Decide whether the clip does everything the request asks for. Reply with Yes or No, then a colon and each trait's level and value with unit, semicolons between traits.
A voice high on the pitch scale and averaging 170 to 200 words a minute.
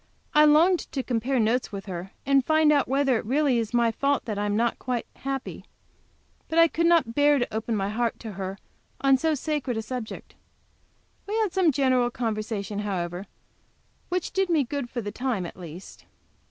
Yes: very high, 250 Hz; average, 195 wpm